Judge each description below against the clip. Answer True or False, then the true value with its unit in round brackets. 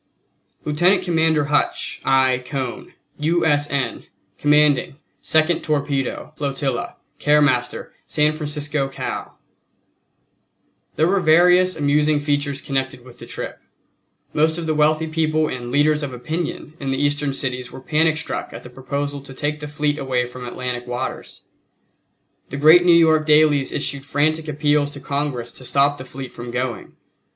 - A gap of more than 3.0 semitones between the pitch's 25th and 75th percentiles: False (2.5 semitones)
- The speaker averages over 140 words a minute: True (150 wpm)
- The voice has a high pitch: False (145 Hz)